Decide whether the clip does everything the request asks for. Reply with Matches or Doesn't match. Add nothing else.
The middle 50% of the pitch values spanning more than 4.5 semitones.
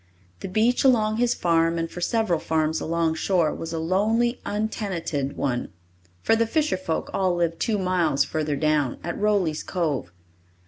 Matches